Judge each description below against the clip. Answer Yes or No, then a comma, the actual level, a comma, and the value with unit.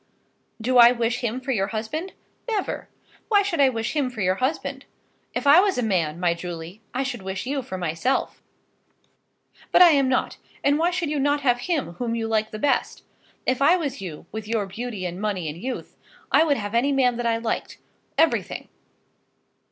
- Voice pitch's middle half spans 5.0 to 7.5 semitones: Yes, average, 5.3 semitones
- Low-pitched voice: No, high, 245 Hz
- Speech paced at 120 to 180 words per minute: No, average, 200 wpm